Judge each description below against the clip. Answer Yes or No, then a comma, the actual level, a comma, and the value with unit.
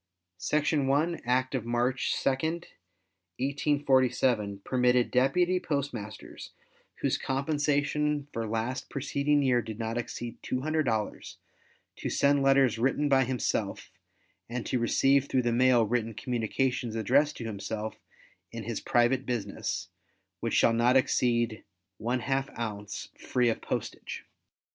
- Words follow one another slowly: Yes, slow, 120 wpm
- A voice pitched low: Yes, low, 125 Hz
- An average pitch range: Yes, average, 3.2 semitones